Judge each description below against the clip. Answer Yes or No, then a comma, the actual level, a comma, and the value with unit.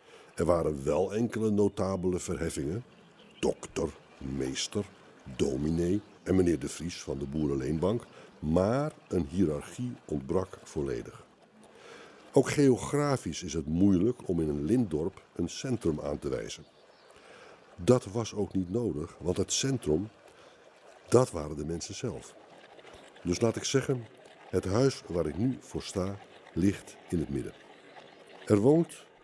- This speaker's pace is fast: No, slow, 135 wpm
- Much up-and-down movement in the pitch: Yes, wide, 6.4 semitones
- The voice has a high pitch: No, very low, 95 Hz